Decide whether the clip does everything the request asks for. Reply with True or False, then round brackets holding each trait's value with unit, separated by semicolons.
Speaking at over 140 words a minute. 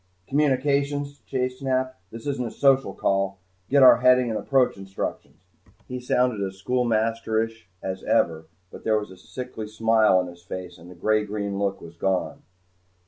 True (165 wpm)